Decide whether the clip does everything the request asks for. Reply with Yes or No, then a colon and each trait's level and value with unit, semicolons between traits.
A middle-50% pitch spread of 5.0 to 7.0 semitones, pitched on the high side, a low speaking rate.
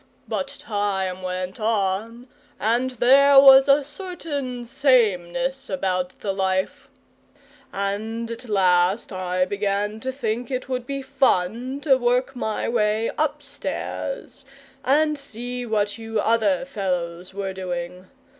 Yes: wide, 5.6 semitones; high, 225 Hz; slow, 120 wpm